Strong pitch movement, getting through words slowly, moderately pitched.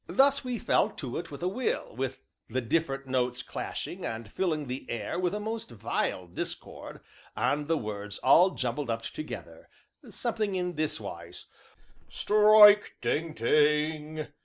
No: wide, 7.5 semitones; average, 145 wpm; medium, 150 Hz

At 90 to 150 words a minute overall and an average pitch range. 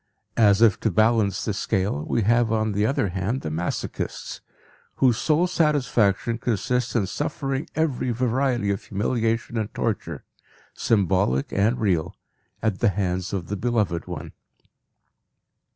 Yes: slow, 135 wpm; average, 3.8 semitones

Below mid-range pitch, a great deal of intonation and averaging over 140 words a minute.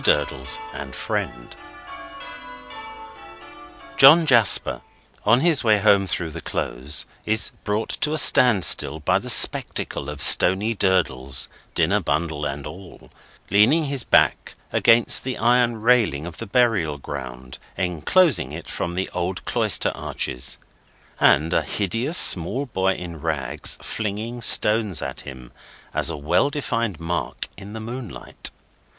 No: low, 100 Hz; wide, 7.1 semitones; slow, 135 wpm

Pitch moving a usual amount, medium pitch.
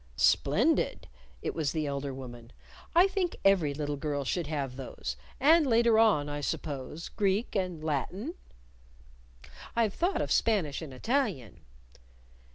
No: wide, 8.0 semitones; medium, 160 Hz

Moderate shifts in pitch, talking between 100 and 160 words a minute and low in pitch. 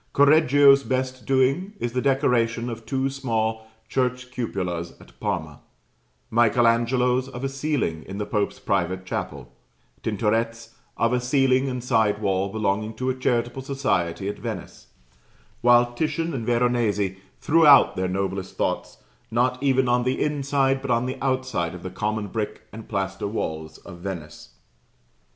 Yes: average, 4.4 semitones; average, 150 wpm; low, 120 Hz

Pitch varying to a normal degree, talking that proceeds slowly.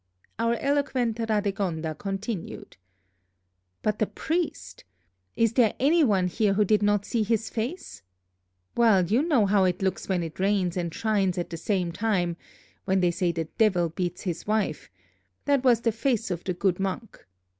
No: average, 4.1 semitones; average, 165 wpm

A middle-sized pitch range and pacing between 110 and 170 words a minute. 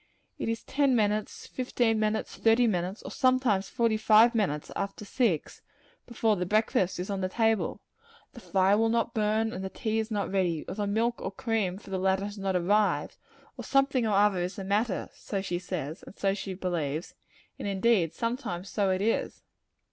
No: average, 3.0 semitones; average, 195 wpm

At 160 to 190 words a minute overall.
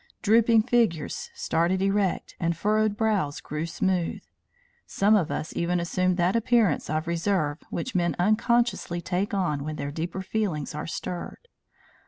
No: average, 145 wpm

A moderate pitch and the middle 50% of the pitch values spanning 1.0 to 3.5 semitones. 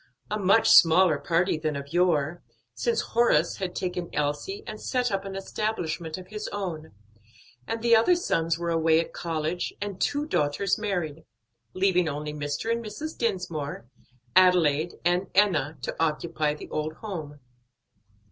No: medium, 175 Hz; average, 4.6 semitones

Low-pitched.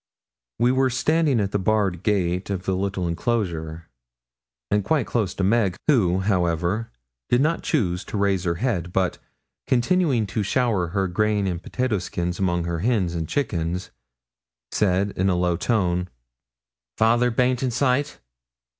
Yes: low, 100 Hz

